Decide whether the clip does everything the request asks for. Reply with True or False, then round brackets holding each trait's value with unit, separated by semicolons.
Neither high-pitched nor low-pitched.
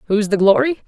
False (220 Hz)